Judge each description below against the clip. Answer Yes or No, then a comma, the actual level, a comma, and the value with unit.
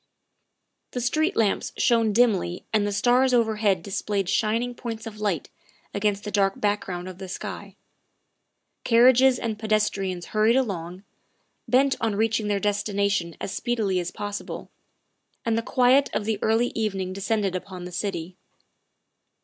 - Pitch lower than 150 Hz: No, high, 210 Hz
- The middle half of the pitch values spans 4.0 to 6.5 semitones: No, average, 2.9 semitones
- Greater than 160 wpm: No, average, 145 wpm